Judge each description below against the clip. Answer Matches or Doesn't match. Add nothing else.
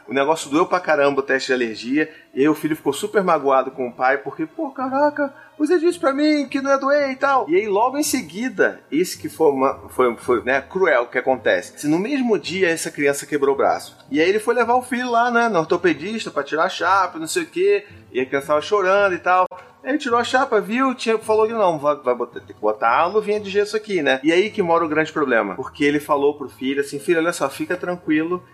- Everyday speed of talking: Doesn't match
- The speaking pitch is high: Matches